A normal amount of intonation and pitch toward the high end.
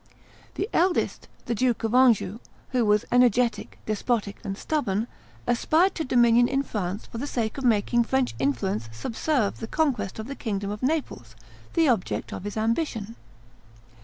Yes: average, 4.1 semitones; high, 230 Hz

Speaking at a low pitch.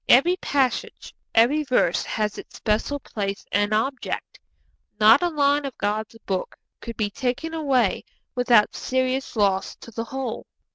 No: high, 245 Hz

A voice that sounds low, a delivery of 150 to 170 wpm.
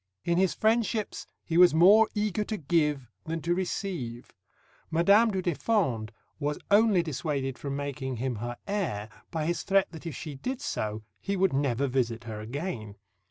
No: medium, 160 Hz; average, 165 wpm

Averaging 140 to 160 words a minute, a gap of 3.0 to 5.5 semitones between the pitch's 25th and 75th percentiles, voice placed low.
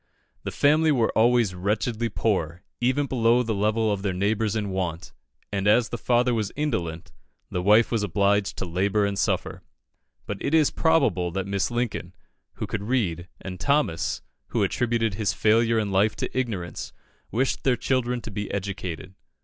No: average, 170 wpm; average, 3.7 semitones; low, 105 Hz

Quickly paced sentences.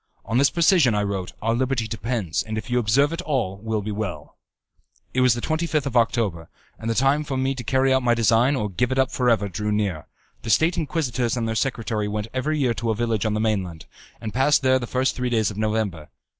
Yes: fast, 240 wpm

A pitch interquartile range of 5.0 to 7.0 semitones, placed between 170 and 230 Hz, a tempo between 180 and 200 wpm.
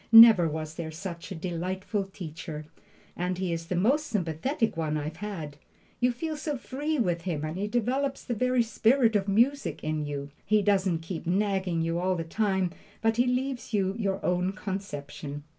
Yes: wide, 5.5 semitones; high, 190 Hz; average, 185 wpm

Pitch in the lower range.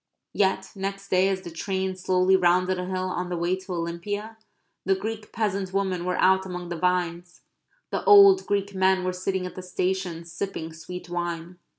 No: medium, 185 Hz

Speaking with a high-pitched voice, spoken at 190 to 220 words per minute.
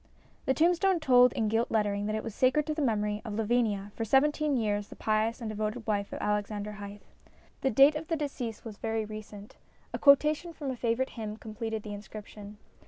Yes: high, 225 Hz; average, 200 wpm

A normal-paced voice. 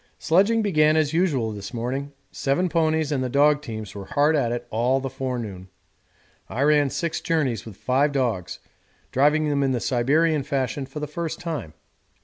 Yes: average, 175 wpm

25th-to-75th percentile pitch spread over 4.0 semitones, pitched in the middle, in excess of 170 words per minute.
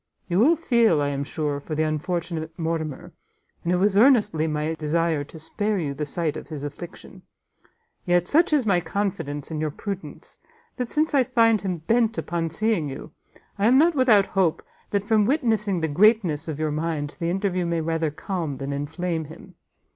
Yes: average, 5.3 semitones; medium, 170 Hz; average, 185 wpm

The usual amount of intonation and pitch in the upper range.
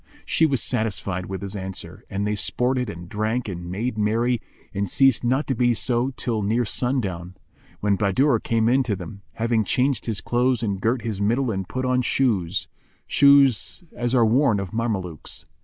No: average, 4.0 semitones; low, 110 Hz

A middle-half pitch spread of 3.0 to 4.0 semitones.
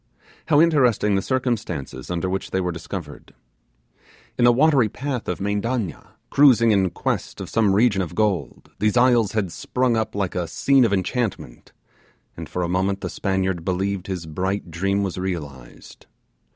No: average, 4.4 semitones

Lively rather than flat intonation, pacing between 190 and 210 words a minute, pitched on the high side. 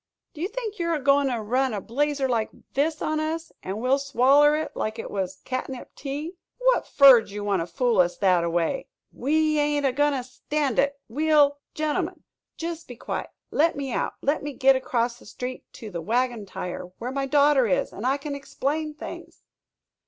No: average, 3.9 semitones; average, 200 wpm; very high, 275 Hz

